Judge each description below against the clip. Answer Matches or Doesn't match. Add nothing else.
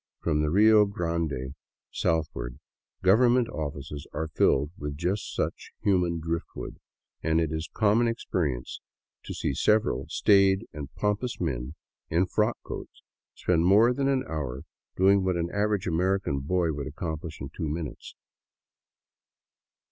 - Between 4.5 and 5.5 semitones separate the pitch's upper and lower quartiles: Matches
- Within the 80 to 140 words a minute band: Matches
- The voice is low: Matches